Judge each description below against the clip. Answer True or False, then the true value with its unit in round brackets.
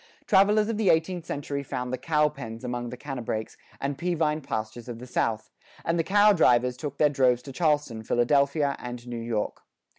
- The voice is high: False (140 Hz)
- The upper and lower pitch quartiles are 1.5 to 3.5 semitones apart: False (4.7 semitones)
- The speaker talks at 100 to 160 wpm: False (180 wpm)